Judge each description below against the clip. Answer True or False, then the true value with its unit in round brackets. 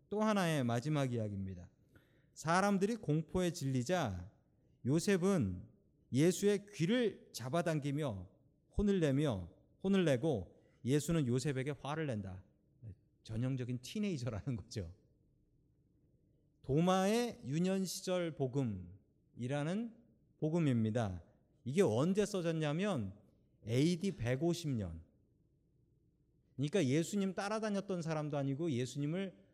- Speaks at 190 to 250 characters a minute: True (240 characters per minute)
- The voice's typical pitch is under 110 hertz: False (145 Hz)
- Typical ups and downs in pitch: False (7.0 semitones)